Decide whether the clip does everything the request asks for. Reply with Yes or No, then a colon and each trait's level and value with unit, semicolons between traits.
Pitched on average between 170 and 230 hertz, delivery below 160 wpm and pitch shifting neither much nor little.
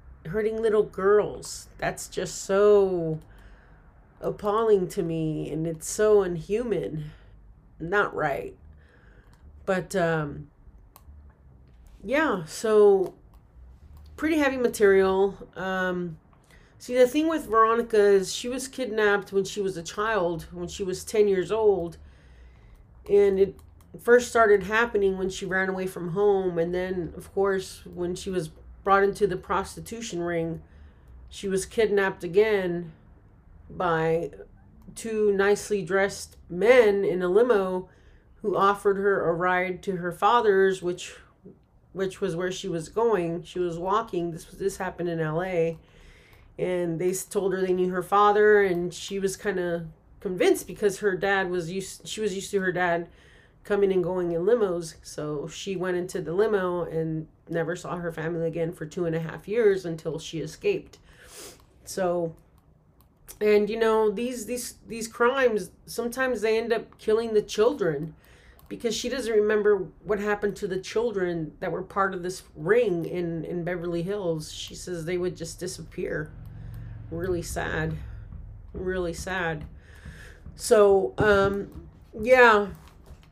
Yes: medium, 185 Hz; average, 145 wpm; average, 3.8 semitones